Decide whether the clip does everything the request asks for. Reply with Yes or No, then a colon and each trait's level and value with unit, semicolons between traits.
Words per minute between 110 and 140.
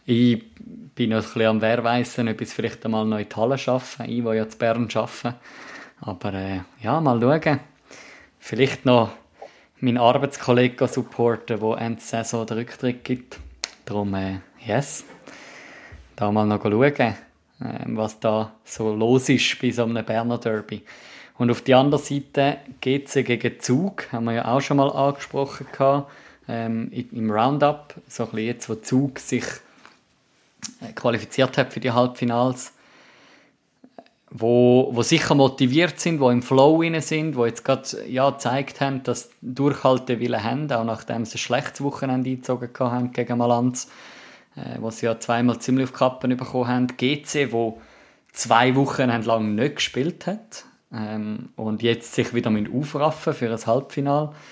No: average, 160 wpm